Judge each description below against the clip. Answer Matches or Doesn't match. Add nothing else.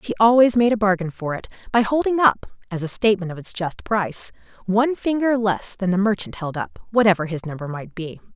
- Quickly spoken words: Matches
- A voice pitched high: Matches